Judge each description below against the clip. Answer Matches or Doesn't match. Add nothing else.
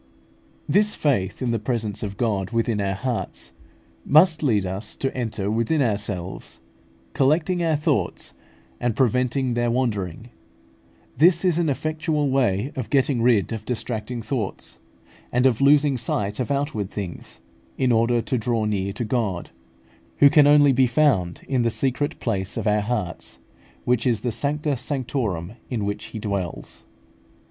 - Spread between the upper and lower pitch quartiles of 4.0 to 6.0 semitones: Matches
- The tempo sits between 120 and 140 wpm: Doesn't match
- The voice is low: Matches